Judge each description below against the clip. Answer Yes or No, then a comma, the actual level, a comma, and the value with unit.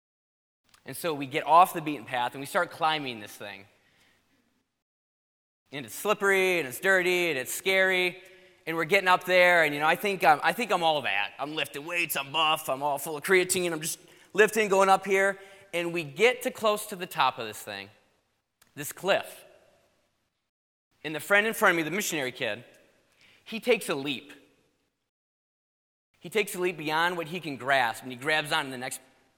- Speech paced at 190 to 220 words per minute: Yes, average, 200 wpm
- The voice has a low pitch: No, medium, 170 Hz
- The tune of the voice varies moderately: Yes, average, 4.9 semitones